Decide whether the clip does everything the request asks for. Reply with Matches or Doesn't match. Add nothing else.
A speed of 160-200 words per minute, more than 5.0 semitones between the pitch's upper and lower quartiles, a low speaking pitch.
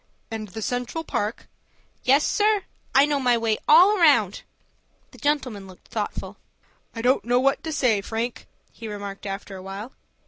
Doesn't match